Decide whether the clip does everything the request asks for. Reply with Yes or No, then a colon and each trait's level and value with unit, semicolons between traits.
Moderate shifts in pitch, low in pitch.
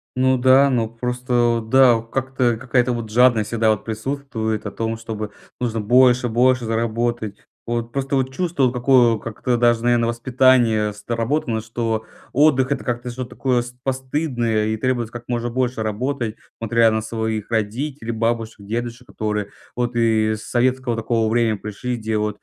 No: narrow, 2.3 semitones; low, 120 Hz